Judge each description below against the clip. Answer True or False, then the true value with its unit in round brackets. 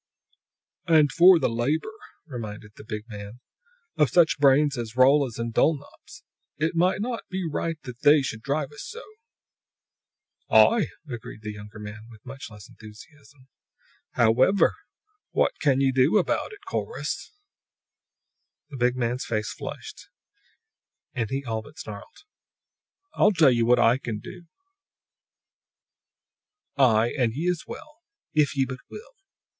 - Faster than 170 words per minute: False (140 wpm)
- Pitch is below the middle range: True (130 Hz)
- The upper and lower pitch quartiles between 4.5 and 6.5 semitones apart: True (5.1 semitones)